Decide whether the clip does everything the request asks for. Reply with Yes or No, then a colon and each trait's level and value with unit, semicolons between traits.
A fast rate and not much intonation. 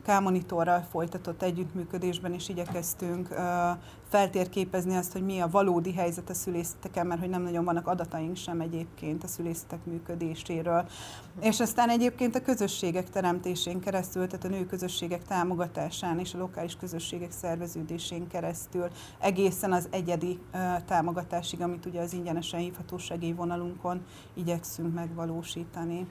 No: average, 125 wpm; narrow, 1.2 semitones